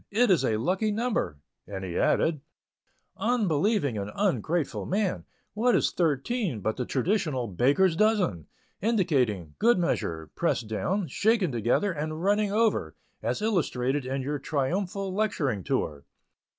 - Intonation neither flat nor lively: No, wide, 8.7 semitones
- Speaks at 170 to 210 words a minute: No, slow, 135 wpm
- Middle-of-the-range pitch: Yes, medium, 165 Hz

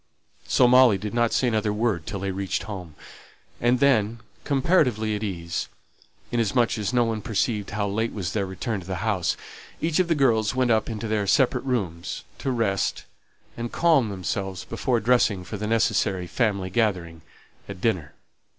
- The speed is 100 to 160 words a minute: No, average, 170 wpm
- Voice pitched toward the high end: No, low, 110 Hz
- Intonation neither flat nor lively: Yes, average, 3.6 semitones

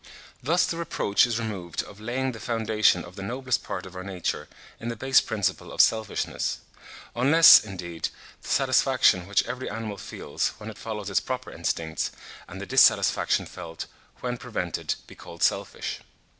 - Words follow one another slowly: No, average, 165 wpm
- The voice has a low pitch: Yes, low, 110 Hz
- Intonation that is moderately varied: Yes, average, 4.6 semitones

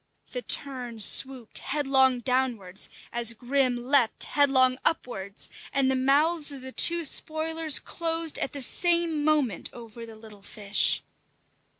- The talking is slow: Yes, slow, 130 wpm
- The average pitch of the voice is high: Yes, very high, 265 Hz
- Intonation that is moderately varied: Yes, average, 4.1 semitones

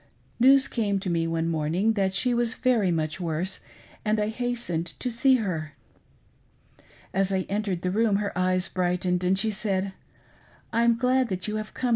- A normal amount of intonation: Yes, average, 4.1 semitones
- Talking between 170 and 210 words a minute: Yes, average, 180 wpm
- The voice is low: No, high, 195 Hz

